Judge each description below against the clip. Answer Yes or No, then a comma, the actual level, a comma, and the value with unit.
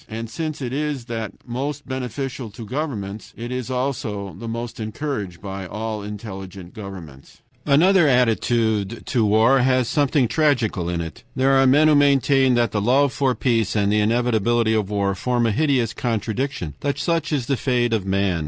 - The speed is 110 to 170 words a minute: No, average, 180 wpm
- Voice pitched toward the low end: Yes, low, 120 Hz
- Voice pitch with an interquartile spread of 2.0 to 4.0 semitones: No, average, 4.4 semitones